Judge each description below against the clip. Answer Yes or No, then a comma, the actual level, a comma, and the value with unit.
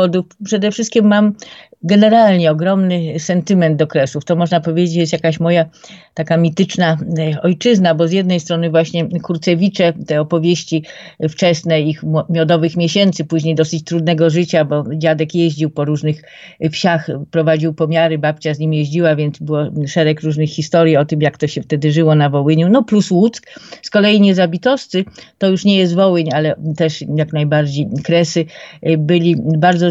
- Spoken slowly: No, average, 155 wpm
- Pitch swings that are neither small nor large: No, narrow, 2.1 semitones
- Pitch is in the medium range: Yes, medium, 165 Hz